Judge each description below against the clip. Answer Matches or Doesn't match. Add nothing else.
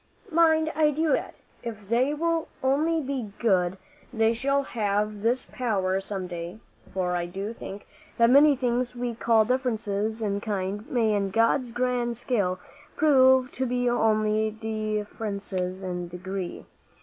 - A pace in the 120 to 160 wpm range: Matches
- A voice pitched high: Matches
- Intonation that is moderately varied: Matches